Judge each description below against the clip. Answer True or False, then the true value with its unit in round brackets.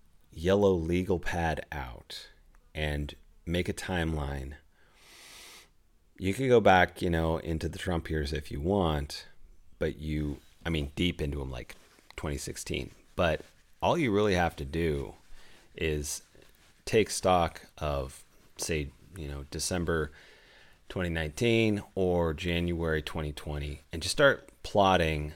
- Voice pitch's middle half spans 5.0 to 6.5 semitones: False (3.1 semitones)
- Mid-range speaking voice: False (80 Hz)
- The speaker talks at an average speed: False (125 wpm)